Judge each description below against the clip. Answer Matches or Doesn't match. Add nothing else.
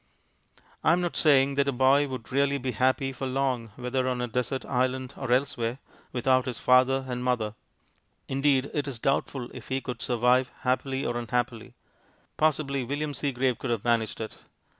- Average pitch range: Doesn't match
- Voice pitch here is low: Matches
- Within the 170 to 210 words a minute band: Matches